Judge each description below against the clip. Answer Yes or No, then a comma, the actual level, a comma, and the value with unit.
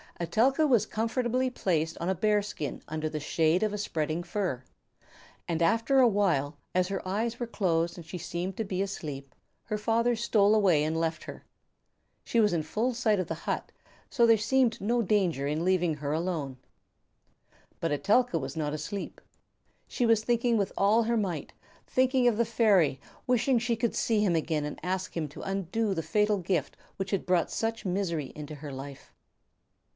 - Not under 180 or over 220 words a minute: Yes, average, 185 wpm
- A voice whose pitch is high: Yes, high, 195 Hz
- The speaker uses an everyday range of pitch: No, wide, 5.7 semitones